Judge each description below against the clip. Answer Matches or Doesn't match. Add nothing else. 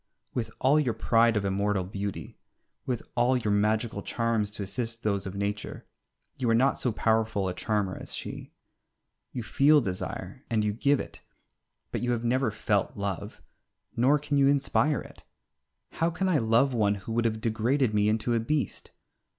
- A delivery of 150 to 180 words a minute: Matches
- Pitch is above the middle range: Doesn't match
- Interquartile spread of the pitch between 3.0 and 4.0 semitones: Matches